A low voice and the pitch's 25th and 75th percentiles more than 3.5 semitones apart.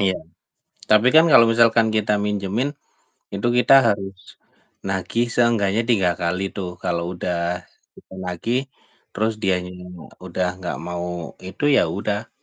Yes: very low, 95 Hz; average, 4.0 semitones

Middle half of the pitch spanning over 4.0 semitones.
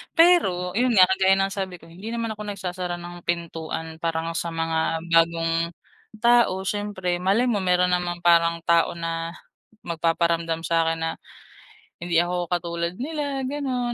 No: average, 3.3 semitones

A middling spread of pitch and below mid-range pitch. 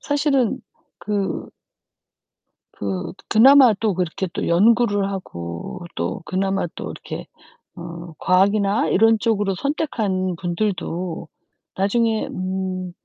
No: average, 3.6 semitones; high, 195 Hz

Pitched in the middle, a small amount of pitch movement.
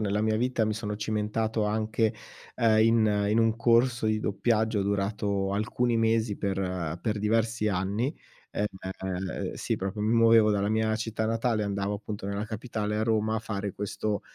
No: low, 110 Hz; narrow, 1.8 semitones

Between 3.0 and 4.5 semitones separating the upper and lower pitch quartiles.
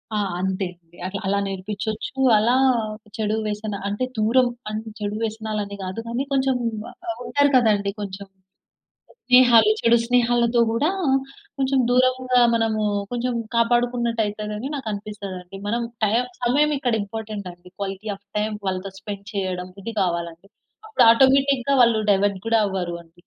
Yes: average, 3.5 semitones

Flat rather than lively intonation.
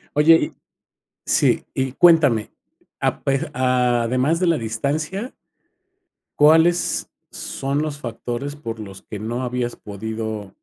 No: average, 5.0 semitones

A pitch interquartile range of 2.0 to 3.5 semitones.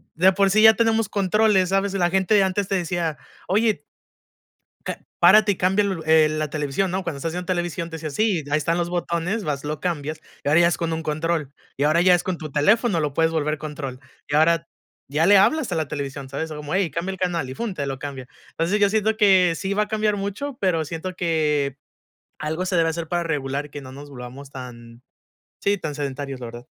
No: average, 4.5 semitones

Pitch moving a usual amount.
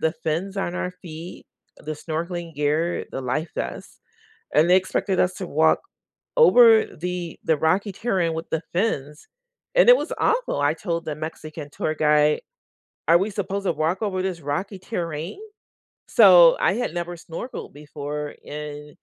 Yes: average, 3.5 semitones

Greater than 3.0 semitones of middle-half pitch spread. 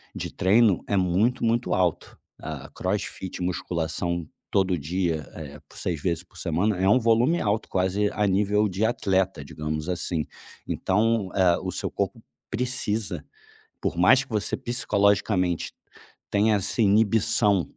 Yes: average, 3.4 semitones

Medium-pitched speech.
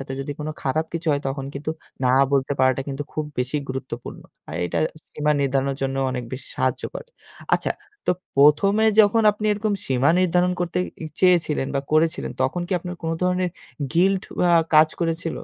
Yes: medium, 155 Hz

